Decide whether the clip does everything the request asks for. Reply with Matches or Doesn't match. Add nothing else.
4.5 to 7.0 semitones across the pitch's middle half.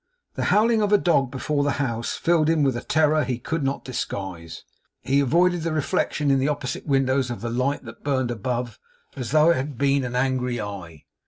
Doesn't match